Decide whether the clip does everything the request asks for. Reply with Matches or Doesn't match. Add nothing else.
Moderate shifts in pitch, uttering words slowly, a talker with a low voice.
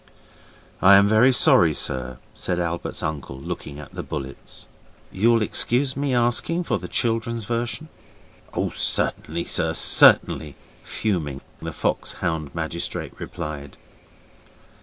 Doesn't match